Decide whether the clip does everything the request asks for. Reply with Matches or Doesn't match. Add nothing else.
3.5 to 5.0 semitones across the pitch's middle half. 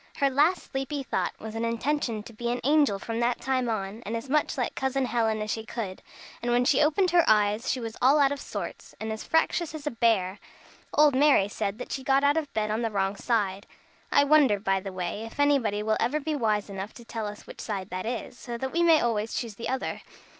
Matches